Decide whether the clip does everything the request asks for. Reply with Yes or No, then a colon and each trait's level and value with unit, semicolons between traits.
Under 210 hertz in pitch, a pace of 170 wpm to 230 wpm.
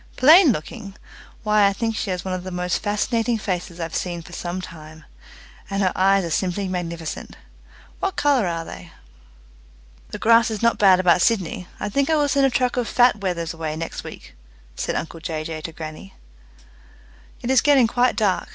Yes: high, 190 Hz; average, 190 wpm